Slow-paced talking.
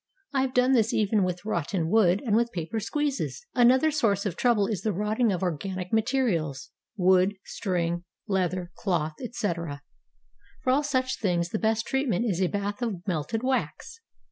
No: average, 170 wpm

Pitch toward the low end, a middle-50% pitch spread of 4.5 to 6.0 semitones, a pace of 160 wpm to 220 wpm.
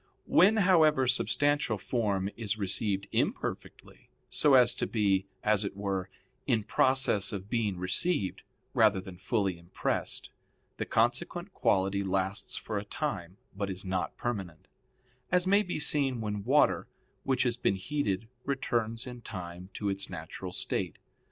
No: low, 105 Hz; average, 5.1 semitones; average, 145 wpm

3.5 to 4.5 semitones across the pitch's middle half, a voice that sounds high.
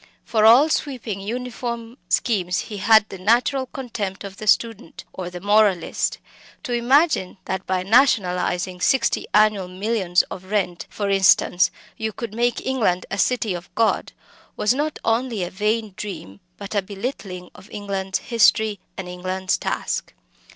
Yes: average, 3.8 semitones; high, 210 Hz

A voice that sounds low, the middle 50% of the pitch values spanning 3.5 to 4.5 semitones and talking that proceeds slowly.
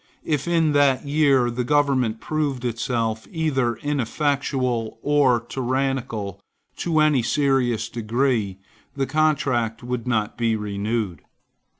Yes: low, 125 Hz; average, 3.8 semitones; slow, 110 wpm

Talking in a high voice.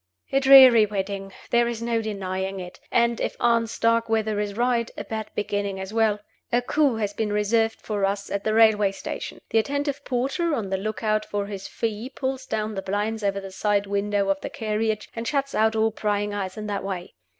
Yes: high, 215 Hz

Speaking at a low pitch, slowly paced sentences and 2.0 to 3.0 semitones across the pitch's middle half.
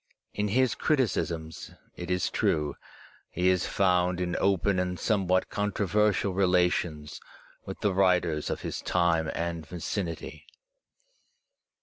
Yes: very low, 90 Hz; slow, 115 wpm; narrow, 2.6 semitones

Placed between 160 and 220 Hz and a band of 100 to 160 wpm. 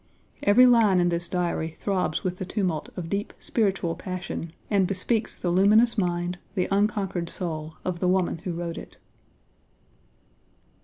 Yes: medium, 185 Hz; average, 150 wpm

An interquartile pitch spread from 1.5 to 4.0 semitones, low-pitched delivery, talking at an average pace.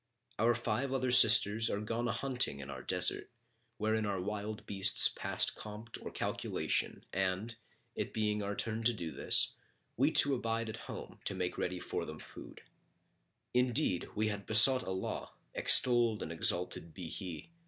Yes: average, 3.4 semitones; low, 110 Hz; average, 165 wpm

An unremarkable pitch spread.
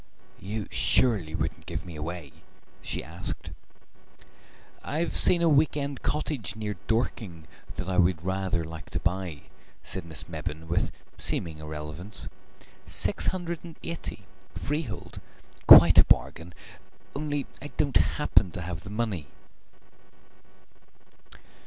No: wide, 9.0 semitones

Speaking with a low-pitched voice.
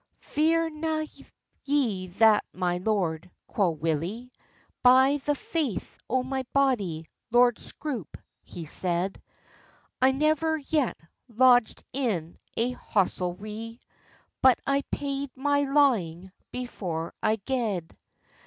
No: high, 240 Hz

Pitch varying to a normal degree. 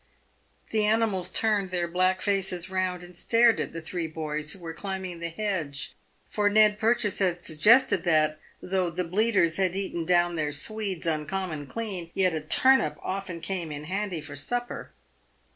Yes: average, 3.6 semitones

